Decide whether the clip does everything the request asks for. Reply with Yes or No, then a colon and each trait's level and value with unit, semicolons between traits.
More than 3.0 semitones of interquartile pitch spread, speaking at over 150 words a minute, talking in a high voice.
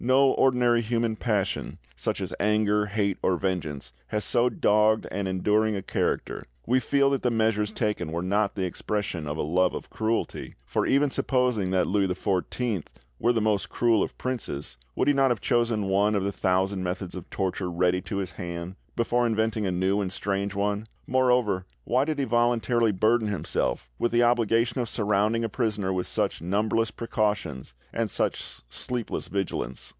No: average, 3.8 semitones; average, 180 wpm; low, 105 Hz